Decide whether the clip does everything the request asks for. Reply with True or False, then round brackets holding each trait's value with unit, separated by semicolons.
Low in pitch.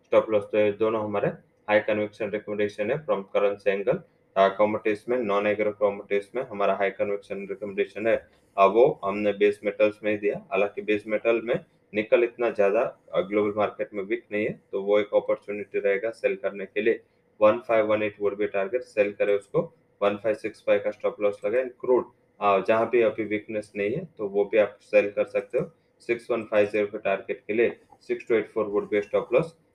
True (115 Hz)